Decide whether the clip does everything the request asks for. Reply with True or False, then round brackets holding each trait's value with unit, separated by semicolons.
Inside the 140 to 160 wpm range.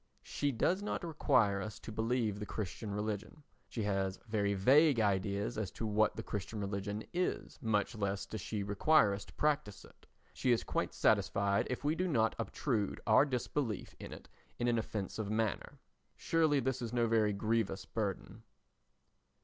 False (170 wpm)